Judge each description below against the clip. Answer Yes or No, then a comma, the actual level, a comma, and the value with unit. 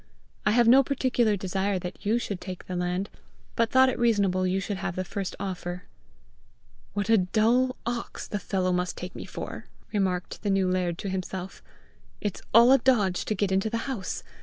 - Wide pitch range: No, average, 3.8 semitones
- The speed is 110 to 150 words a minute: No, average, 185 wpm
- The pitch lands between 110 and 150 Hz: No, high, 195 Hz